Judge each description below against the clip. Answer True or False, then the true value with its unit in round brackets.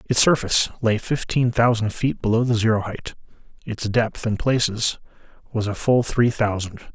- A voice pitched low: True (115 Hz)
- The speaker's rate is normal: True (165 wpm)